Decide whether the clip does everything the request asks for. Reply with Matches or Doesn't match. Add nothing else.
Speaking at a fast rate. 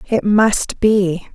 Doesn't match